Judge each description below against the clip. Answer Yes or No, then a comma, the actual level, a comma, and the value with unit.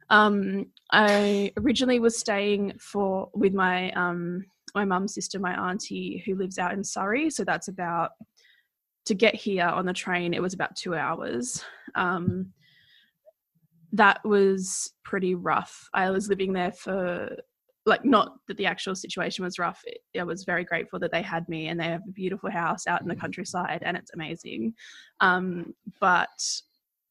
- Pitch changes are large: No, narrow, 2.6 semitones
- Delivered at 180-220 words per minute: No, average, 165 wpm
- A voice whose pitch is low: No, high, 190 Hz